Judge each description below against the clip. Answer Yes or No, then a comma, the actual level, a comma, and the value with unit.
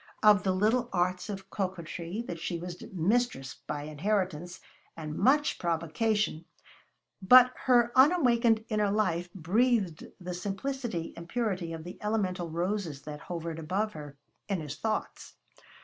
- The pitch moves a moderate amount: Yes, average, 4.6 semitones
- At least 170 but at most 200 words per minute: No, slow, 135 wpm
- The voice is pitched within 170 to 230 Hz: Yes, medium, 185 Hz